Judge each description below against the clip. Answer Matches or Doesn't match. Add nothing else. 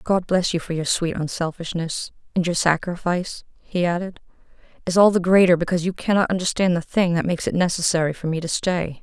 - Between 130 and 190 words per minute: Doesn't match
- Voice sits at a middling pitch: Matches